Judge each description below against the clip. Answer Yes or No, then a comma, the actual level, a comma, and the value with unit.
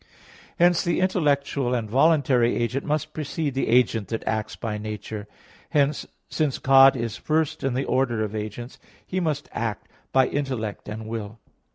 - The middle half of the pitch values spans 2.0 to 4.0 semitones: No, average, 4.8 semitones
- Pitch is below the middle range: Yes, low, 130 Hz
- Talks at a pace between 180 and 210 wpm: No, average, 160 wpm